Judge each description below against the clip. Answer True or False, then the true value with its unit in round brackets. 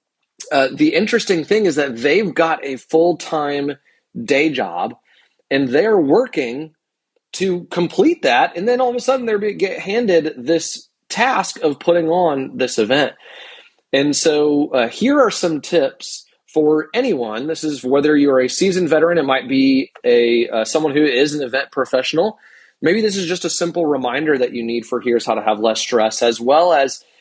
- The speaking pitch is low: False (160 Hz)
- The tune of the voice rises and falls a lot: True (6.0 semitones)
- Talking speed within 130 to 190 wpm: True (185 wpm)